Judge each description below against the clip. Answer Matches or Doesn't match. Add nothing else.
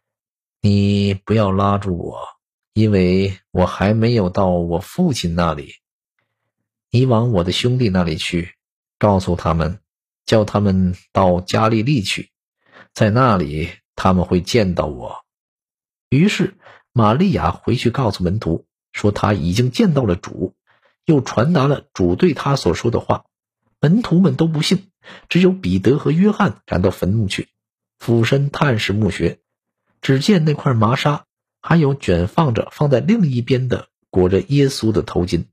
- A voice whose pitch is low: Matches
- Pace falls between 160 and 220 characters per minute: Matches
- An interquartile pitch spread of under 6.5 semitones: Doesn't match